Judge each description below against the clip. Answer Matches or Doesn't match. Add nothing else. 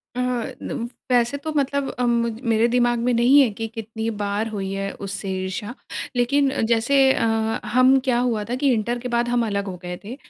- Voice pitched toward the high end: Matches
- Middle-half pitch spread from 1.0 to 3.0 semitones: Matches